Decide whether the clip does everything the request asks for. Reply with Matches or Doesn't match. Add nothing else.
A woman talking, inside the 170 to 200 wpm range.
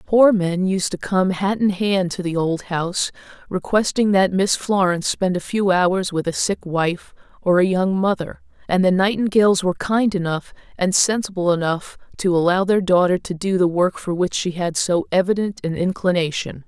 Matches